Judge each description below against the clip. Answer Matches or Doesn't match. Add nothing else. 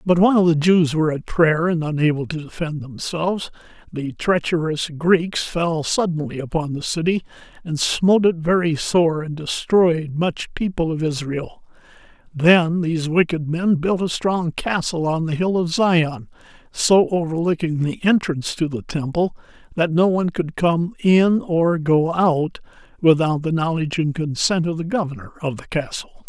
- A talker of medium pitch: Matches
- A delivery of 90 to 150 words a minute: Doesn't match